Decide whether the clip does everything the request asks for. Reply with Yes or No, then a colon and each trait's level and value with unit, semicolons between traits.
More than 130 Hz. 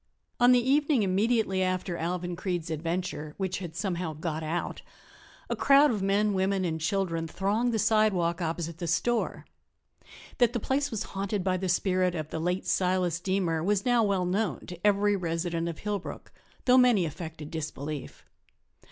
Yes: medium, 185 Hz